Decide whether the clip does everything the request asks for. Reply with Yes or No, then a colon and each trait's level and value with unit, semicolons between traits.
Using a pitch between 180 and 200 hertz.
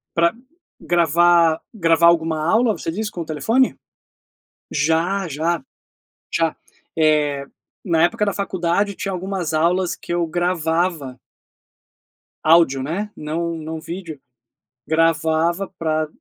No: medium, 170 Hz